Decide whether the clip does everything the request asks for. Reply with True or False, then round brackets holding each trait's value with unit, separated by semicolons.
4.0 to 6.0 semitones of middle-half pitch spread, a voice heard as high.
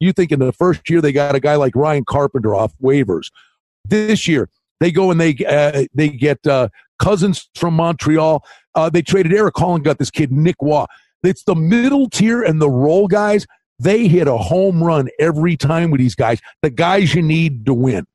False (4.3 semitones; 160 Hz)